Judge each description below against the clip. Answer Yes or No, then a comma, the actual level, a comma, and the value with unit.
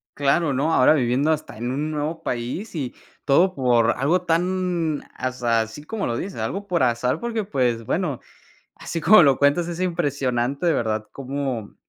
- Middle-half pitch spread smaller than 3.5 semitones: No, wide, 5.5 semitones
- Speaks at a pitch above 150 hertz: No, medium, 145 Hz